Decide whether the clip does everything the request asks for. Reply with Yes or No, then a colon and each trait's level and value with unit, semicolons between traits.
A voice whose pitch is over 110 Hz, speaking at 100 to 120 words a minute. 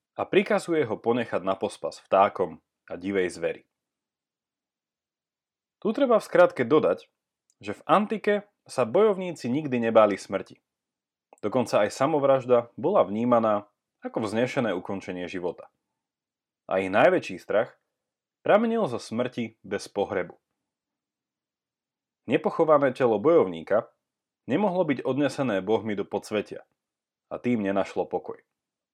Yes: low, 120 Hz; slow, 110 wpm